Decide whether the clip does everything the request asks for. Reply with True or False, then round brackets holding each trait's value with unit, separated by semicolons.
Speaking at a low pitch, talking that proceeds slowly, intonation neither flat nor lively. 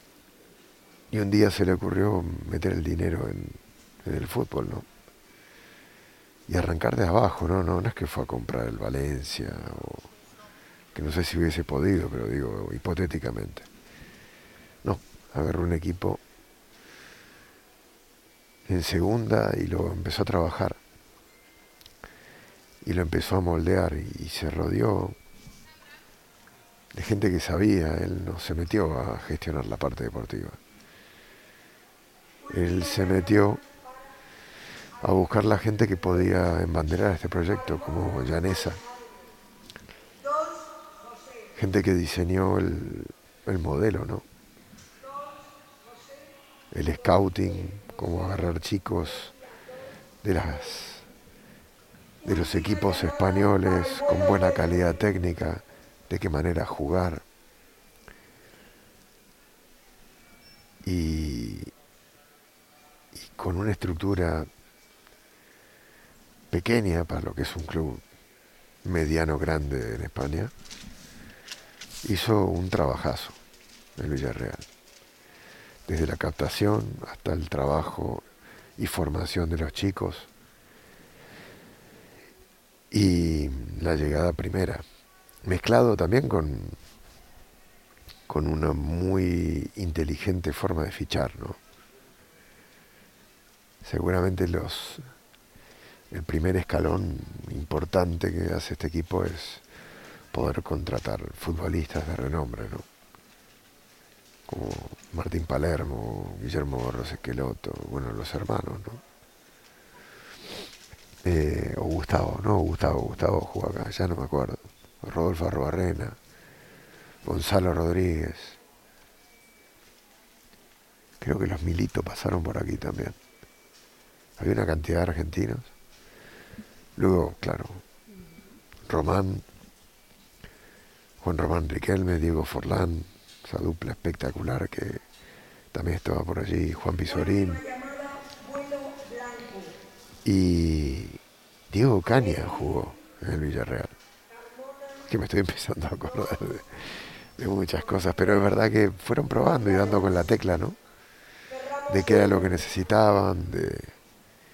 True (90 Hz; 105 wpm; 3.8 semitones)